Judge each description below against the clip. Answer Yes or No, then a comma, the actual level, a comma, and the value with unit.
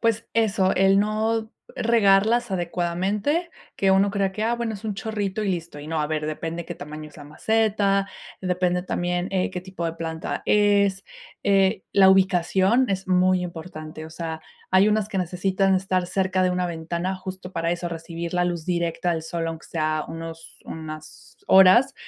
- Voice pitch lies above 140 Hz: Yes, medium, 185 Hz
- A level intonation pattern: No, average, 3.0 semitones